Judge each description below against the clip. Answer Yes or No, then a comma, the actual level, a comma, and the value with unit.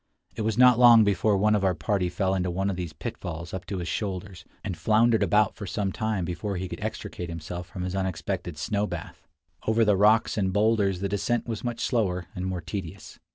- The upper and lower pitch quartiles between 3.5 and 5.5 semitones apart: No, average, 3.1 semitones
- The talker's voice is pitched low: Yes, very low, 95 Hz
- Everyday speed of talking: No, fast, 215 wpm